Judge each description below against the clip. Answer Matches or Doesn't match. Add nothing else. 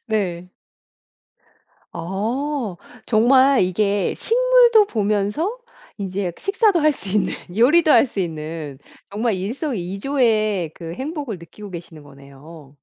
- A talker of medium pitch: Doesn't match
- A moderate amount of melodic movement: Doesn't match